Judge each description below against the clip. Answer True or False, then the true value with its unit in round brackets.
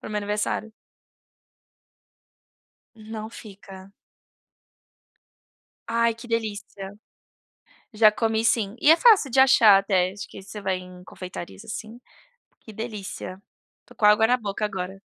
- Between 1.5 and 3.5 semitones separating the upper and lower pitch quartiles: True (2.6 semitones)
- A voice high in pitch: True (210 Hz)